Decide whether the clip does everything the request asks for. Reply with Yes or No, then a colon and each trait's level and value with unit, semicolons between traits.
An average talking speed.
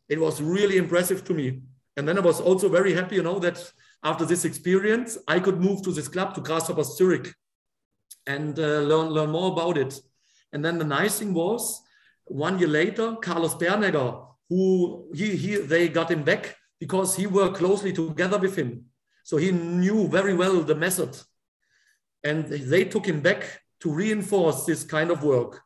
Yes: average, 180 wpm